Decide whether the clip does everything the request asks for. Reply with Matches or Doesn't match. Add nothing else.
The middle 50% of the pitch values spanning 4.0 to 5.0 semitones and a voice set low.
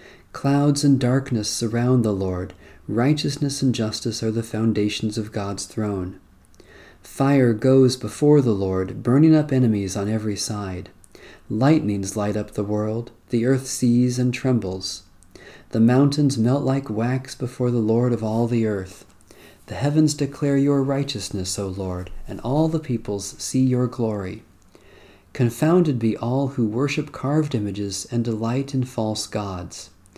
Matches